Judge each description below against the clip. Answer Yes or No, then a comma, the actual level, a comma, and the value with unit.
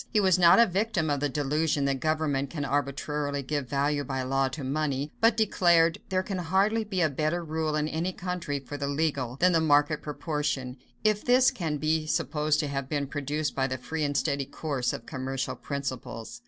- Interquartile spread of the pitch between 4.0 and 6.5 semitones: No, average, 3.0 semitones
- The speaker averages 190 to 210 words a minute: Yes, average, 200 wpm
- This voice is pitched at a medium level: Yes, medium, 150 Hz